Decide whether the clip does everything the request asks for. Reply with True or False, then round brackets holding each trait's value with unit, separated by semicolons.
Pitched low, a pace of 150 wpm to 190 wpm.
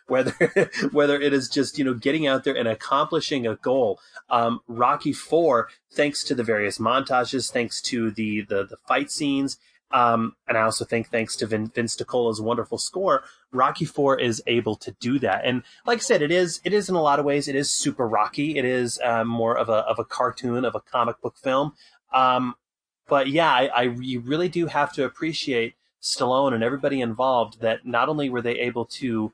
False (125 Hz; 205 wpm)